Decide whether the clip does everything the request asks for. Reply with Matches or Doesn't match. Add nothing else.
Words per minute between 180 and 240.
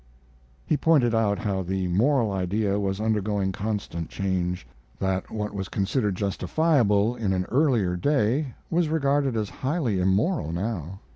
Doesn't match